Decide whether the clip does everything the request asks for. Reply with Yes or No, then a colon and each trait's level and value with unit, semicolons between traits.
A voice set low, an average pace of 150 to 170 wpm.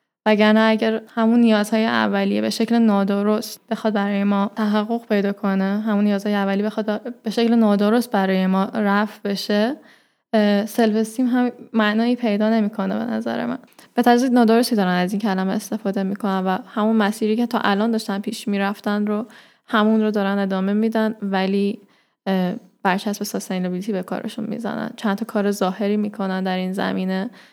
No: high, 210 Hz; fast, 155 wpm